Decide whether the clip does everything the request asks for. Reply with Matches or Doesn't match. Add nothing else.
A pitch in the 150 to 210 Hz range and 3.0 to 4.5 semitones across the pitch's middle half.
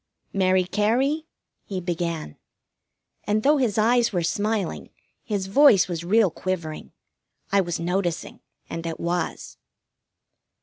Matches